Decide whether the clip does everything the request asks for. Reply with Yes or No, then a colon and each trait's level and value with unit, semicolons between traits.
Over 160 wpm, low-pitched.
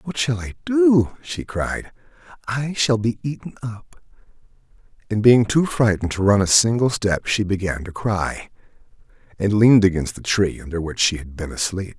Yes: average, 175 wpm; low, 105 Hz